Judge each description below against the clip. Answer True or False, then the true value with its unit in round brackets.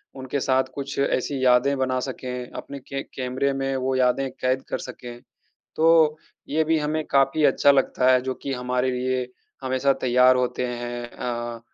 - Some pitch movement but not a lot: False (1.6 semitones)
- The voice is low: True (130 Hz)